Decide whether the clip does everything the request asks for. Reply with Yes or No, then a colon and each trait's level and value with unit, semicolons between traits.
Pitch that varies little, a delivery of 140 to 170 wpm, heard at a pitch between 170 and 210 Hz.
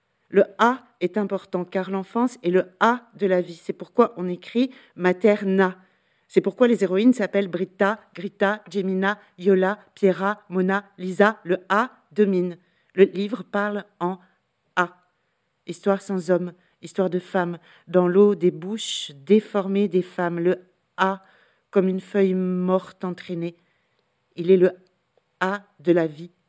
Yes: narrow, 2.1 semitones; slow, 145 wpm; high, 190 Hz